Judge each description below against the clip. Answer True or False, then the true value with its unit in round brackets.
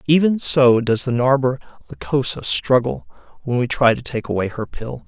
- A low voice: True (130 Hz)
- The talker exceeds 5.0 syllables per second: False (4.8 syllables/s)